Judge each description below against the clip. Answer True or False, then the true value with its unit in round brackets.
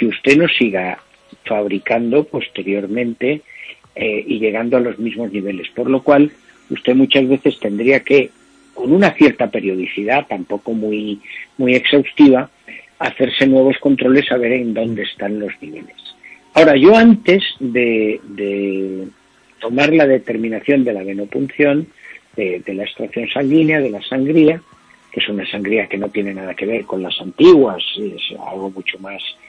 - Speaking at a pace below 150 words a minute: False (155 wpm)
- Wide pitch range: False (4.9 semitones)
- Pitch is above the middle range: False (120 Hz)